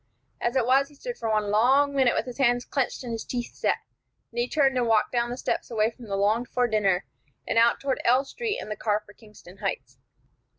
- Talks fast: Yes, fast, 240 wpm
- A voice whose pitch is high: Yes, high, 240 Hz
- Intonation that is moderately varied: Yes, average, 3.5 semitones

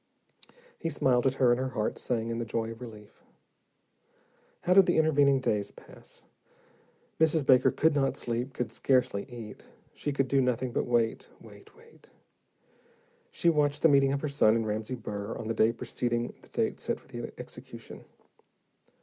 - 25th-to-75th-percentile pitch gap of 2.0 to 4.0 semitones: Yes, average, 3.4 semitones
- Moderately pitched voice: No, low, 125 Hz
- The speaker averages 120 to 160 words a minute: No, average, 175 wpm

